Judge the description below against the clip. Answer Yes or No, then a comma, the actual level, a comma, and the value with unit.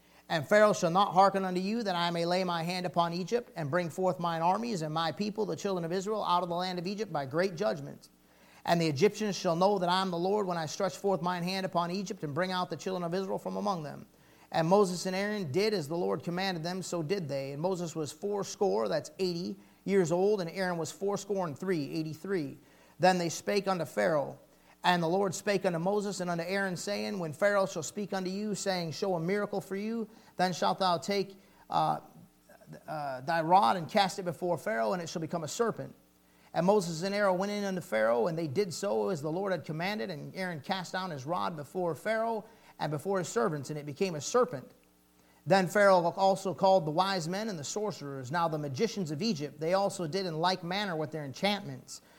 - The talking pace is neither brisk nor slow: No, fast, 225 wpm